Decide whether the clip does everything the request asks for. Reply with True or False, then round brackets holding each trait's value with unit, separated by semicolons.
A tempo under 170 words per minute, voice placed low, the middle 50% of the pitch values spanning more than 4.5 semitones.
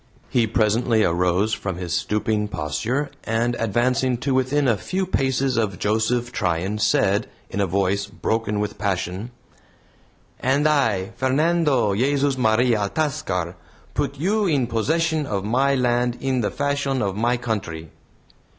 True (140 wpm; 115 Hz; 4.9 semitones)